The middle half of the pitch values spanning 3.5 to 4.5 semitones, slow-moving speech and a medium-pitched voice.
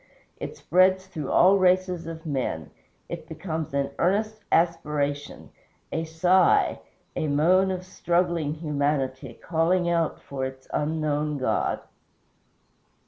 Yes: average, 3.9 semitones; slow, 115 wpm; medium, 160 Hz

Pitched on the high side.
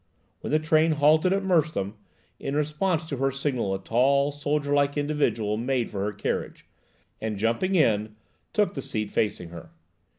No: medium, 140 Hz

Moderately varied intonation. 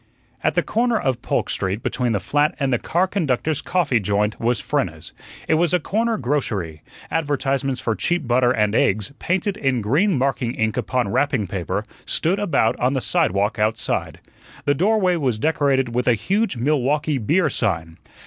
No: wide, 6.2 semitones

